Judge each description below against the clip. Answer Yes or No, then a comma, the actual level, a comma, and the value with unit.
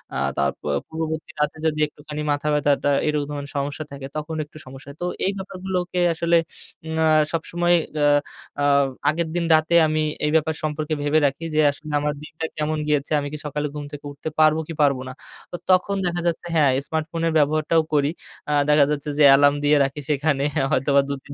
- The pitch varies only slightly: Yes, narrow, 1.8 semitones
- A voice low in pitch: No, medium, 150 Hz